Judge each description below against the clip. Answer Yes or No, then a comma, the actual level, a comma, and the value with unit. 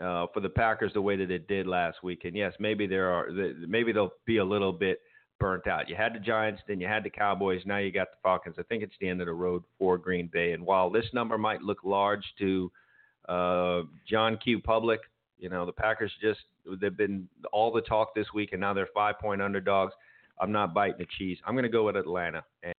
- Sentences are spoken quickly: Yes, fast, 240 wpm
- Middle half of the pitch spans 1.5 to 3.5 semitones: Yes, average, 2.7 semitones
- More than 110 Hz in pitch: No, low, 100 Hz